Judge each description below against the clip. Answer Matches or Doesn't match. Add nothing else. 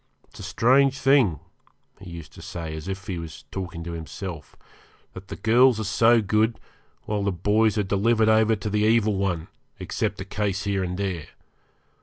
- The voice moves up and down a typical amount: Matches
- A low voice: Matches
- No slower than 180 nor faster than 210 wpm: Matches